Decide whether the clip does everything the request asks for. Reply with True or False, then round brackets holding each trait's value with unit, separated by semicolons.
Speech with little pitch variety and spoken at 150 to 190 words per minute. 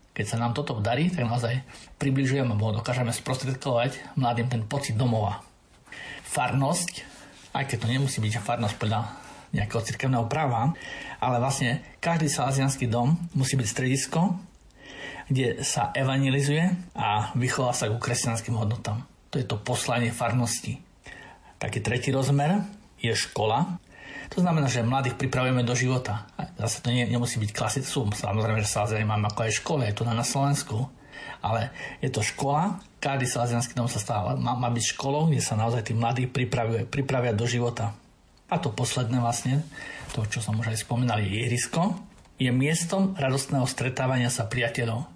False (3.1 semitones; 155 wpm)